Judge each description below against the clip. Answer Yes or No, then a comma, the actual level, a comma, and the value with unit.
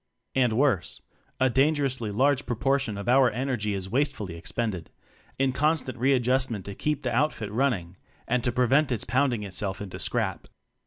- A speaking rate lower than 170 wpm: Yes, average, 155 wpm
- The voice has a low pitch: Yes, low, 125 Hz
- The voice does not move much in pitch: No, average, 4.3 semitones